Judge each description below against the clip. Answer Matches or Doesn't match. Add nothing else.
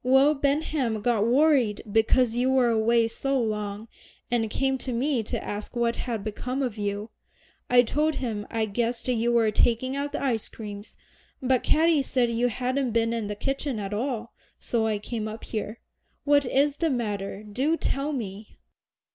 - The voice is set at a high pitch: Matches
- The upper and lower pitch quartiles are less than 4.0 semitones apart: Matches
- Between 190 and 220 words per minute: Doesn't match